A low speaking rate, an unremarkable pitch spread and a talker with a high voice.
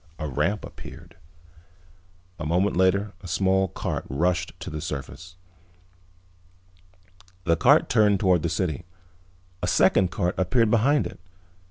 No: slow, 130 wpm; average, 3.0 semitones; very low, 90 Hz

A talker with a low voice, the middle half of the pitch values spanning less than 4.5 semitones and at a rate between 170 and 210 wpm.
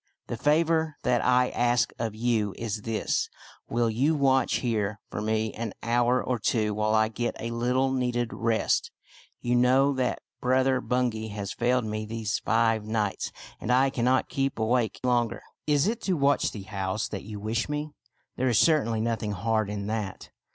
Yes: low, 115 Hz; average, 2.8 semitones; average, 180 wpm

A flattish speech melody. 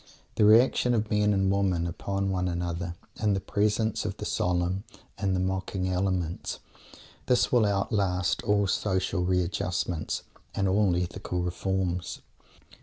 Yes: narrow, 2.2 semitones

